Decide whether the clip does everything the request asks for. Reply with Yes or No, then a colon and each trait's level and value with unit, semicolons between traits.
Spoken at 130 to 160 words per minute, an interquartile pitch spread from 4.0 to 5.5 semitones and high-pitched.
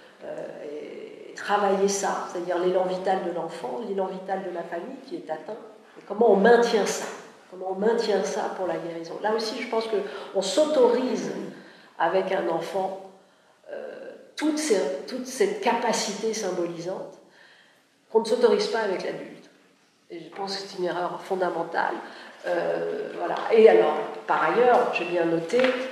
Yes: average, 155 wpm; average, 4.9 semitones; high, 200 Hz